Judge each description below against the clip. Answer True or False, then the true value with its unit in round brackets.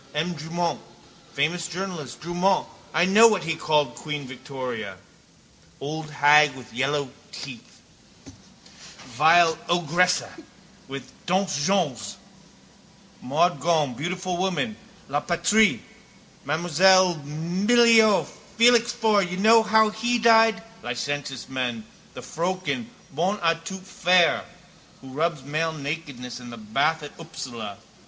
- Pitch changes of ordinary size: True (4.8 semitones)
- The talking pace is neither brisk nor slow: False (115 wpm)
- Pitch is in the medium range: True (165 Hz)